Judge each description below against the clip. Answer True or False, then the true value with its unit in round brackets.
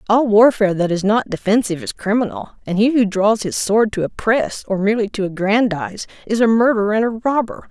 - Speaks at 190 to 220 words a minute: True (200 wpm)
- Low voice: False (215 Hz)